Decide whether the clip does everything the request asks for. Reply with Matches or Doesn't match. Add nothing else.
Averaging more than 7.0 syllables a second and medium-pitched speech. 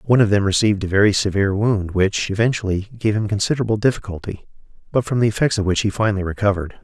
Doesn't match